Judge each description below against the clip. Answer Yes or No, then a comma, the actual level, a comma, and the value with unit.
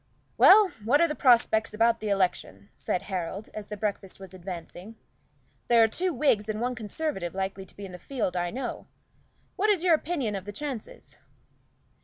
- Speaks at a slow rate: No, average, 180 wpm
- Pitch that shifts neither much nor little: No, wide, 5.8 semitones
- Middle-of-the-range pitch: No, high, 215 Hz